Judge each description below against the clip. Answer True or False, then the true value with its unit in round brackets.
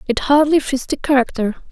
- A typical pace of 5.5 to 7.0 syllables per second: True (5.6 syllables/s)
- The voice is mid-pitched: False (270 Hz)